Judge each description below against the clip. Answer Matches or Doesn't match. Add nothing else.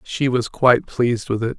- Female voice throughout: Doesn't match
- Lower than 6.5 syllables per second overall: Matches